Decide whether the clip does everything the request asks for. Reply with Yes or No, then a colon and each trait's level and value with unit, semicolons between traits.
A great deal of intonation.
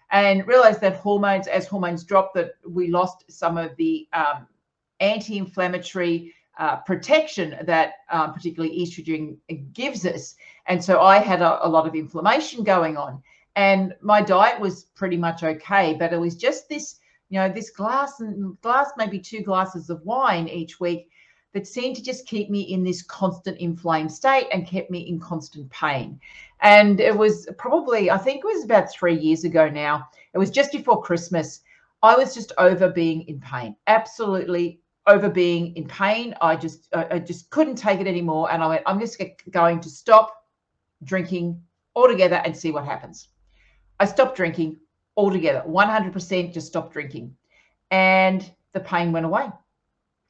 No: average, 3.8 semitones